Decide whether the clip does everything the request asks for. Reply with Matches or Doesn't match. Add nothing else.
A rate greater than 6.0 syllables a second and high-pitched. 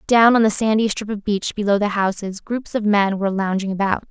Doesn't match